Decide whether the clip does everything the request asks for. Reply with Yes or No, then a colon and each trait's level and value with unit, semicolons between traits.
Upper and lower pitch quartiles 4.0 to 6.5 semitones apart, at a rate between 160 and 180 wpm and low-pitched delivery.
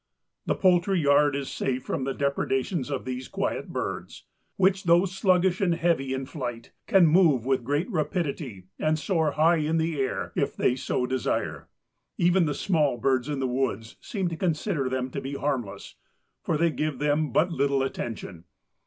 No: average, 4.4 semitones; average, 175 wpm; medium, 145 Hz